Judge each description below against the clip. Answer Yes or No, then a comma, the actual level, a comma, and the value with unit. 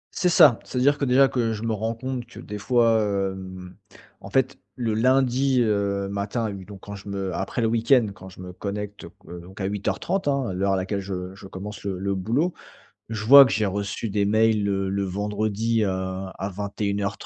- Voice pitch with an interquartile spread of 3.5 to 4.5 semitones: No, average, 3.0 semitones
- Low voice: Yes, low, 105 Hz